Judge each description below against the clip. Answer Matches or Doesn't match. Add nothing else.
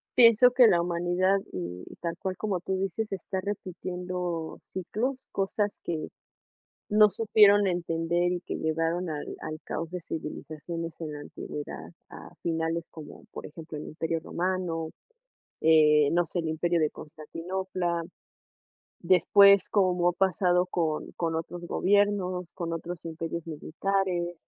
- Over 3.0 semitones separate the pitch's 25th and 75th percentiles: Doesn't match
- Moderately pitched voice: Matches